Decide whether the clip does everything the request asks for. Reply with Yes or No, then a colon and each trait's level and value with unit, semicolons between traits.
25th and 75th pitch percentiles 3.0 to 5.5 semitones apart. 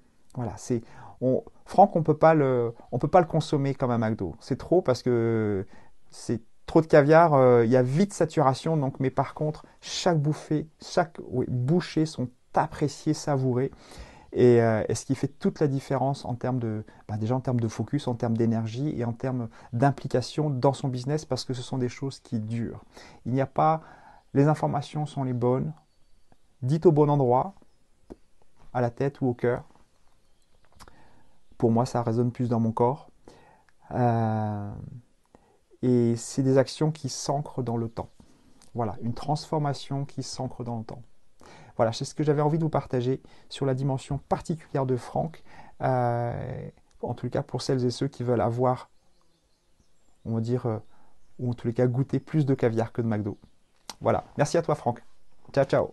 Yes: average, 3.4 semitones